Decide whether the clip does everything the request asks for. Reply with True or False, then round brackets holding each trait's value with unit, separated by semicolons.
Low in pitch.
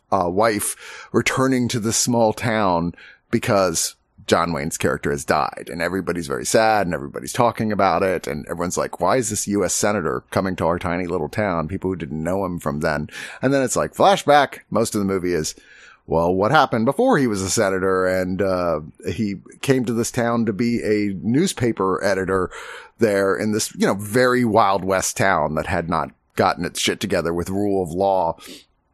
True (95 Hz)